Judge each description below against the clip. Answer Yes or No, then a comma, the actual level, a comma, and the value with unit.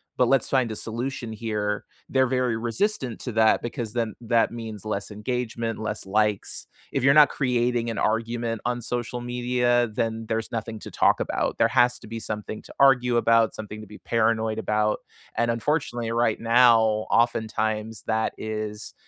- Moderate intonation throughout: No, narrow, 1.9 semitones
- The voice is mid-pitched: No, low, 115 Hz